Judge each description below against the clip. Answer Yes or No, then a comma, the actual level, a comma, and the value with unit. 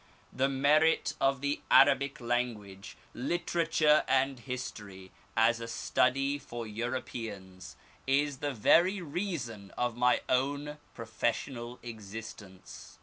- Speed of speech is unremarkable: No, slow, 105 wpm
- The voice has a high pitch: No, low, 125 Hz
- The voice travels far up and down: No, average, 3.9 semitones